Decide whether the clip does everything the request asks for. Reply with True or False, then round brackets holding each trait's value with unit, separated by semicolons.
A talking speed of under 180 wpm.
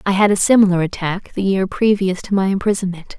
False (205 wpm)